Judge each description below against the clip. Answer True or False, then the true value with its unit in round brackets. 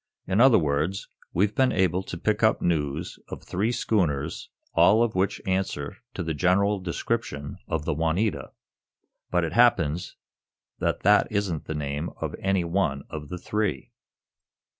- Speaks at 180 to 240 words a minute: False (155 wpm)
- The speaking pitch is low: True (90 Hz)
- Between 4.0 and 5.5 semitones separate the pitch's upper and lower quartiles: True (4.6 semitones)